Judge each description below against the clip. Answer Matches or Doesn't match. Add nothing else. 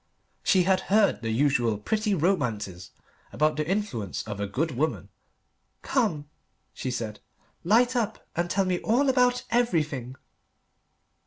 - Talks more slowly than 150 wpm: Matches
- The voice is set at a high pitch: Doesn't match